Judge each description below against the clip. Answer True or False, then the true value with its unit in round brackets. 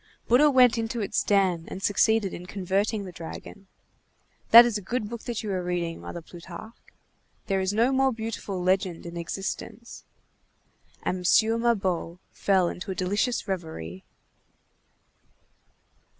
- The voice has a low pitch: False (195 Hz)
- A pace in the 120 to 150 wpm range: True (140 wpm)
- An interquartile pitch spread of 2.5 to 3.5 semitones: False (4.0 semitones)